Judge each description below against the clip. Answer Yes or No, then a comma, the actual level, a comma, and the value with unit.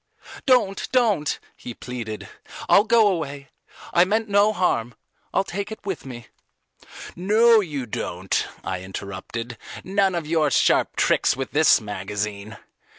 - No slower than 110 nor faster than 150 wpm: Yes, slow, 135 wpm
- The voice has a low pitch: No, medium, 155 Hz